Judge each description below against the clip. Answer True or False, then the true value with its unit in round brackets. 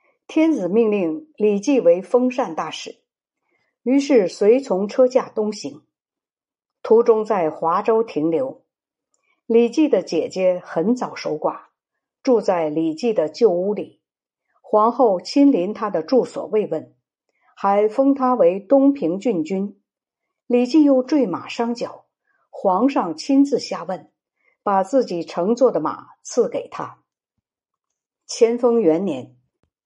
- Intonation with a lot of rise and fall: True (5.9 semitones)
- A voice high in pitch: True (230 Hz)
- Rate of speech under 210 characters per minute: True (175 characters per minute)